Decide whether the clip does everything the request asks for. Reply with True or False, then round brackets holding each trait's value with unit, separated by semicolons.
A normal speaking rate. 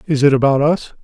False (230 wpm)